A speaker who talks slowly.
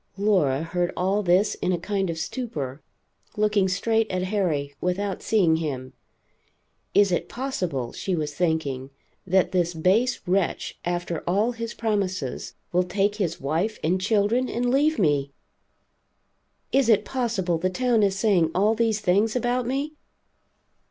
No: average, 145 wpm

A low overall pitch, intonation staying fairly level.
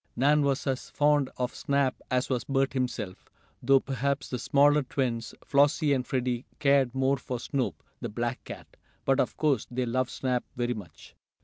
Yes: low, 130 Hz; narrow, 2.1 semitones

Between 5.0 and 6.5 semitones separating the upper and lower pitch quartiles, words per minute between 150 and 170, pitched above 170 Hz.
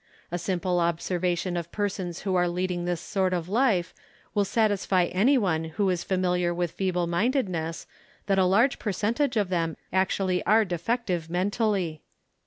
No: average, 2.8 semitones; average, 165 wpm; medium, 185 Hz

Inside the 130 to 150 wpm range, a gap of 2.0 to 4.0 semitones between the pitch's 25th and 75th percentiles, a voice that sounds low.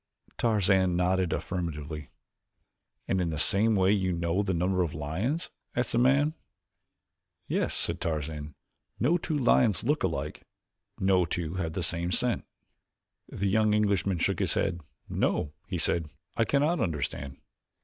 No: average, 145 wpm; average, 4.6 semitones; very low, 95 Hz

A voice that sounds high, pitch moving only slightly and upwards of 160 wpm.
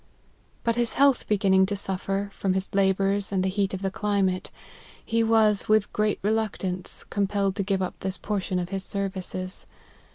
Yes: high, 195 Hz; narrow, 1.7 semitones; average, 175 wpm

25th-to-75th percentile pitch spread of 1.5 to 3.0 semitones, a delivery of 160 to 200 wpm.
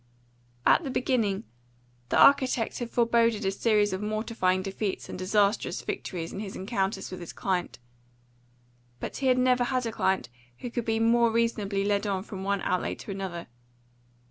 No: average, 3.4 semitones; average, 170 wpm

